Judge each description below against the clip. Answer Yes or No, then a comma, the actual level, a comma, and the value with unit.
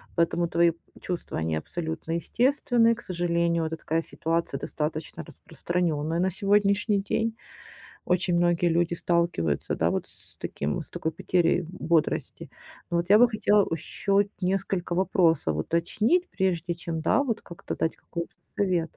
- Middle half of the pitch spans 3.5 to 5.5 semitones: No, average, 3.0 semitones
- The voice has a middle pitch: Yes, medium, 175 Hz